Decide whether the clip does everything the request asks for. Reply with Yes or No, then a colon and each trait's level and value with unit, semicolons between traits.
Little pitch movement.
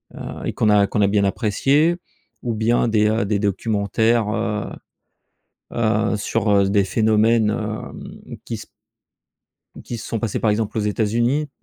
Yes: narrow, 1.8 semitones